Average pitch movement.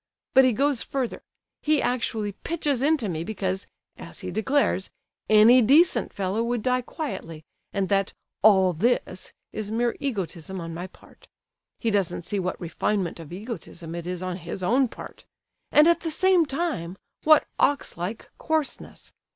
No: wide, 6.6 semitones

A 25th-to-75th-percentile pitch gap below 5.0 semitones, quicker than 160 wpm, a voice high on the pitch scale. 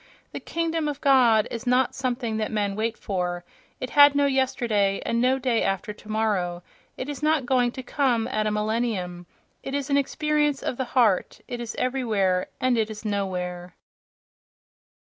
Yes: average, 4.2 semitones; average, 170 wpm; high, 235 Hz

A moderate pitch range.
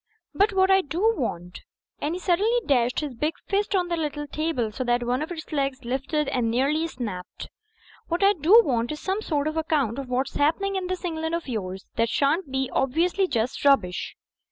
No: wide, 5.8 semitones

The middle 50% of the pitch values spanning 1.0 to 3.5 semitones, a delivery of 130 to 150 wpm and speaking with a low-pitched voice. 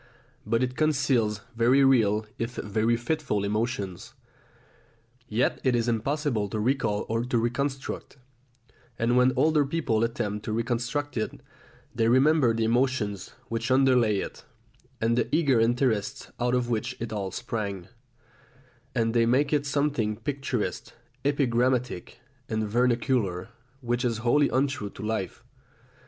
Yes: average, 3.2 semitones; slow, 135 wpm; low, 120 Hz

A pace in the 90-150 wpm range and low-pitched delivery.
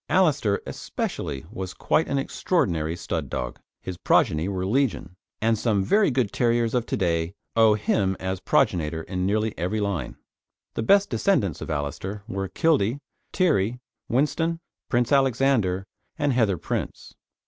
Yes: average, 145 wpm; low, 105 Hz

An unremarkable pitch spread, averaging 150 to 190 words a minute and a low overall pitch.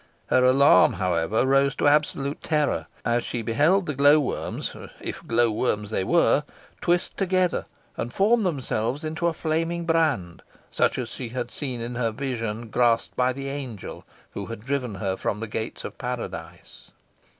Yes: average, 4.9 semitones; average, 165 wpm; low, 130 Hz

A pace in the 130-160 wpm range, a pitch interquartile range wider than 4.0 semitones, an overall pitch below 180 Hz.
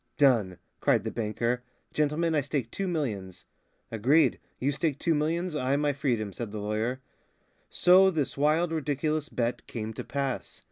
Yes: average, 155 wpm; average, 4.9 semitones; medium, 140 Hz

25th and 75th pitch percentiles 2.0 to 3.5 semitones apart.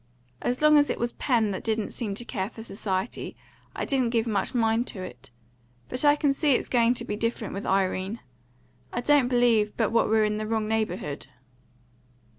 Yes: average, 2.7 semitones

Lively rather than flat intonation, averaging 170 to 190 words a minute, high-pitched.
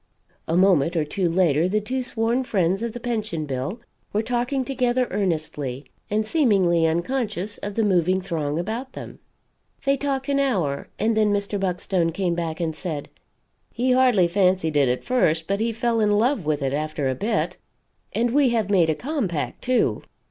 Yes: wide, 6.3 semitones; average, 180 wpm; high, 200 Hz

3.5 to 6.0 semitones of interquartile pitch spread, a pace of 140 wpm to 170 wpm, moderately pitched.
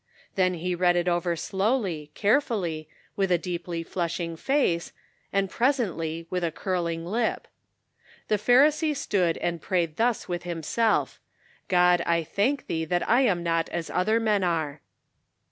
Yes: average, 4.0 semitones; average, 155 wpm; medium, 180 Hz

